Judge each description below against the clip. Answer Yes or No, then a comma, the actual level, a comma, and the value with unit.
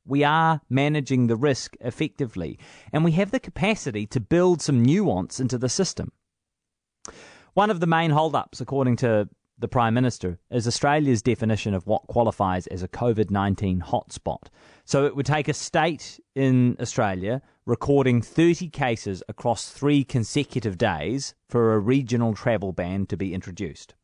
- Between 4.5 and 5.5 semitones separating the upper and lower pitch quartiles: Yes, average, 5.1 semitones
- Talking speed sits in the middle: Yes, average, 150 wpm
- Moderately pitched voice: No, low, 125 Hz